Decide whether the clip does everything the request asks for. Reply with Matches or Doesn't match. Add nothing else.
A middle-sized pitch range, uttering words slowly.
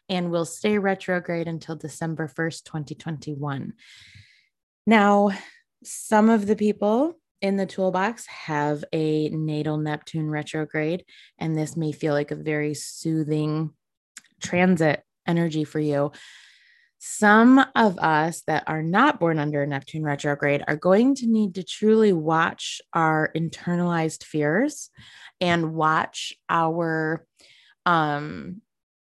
Matches